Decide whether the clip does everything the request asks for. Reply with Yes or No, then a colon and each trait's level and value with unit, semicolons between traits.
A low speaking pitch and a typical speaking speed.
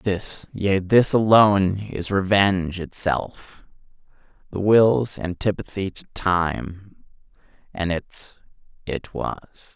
No: very low, 95 Hz; slow, 100 wpm